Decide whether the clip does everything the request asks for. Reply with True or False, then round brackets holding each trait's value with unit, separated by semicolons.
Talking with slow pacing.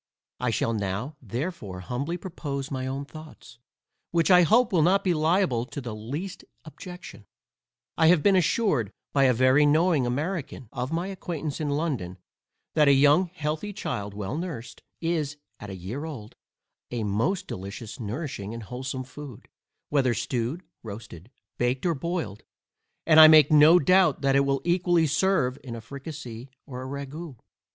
False (160 wpm)